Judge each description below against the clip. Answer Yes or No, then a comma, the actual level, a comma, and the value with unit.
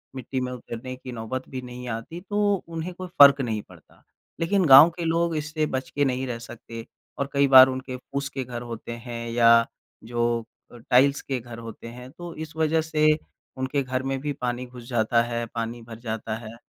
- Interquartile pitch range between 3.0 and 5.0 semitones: Yes, average, 3.6 semitones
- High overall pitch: No, low, 130 Hz